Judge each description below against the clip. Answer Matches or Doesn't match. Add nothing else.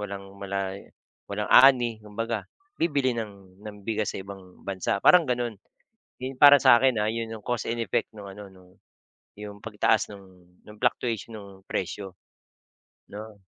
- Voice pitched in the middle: Doesn't match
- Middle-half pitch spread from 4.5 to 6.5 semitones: Doesn't match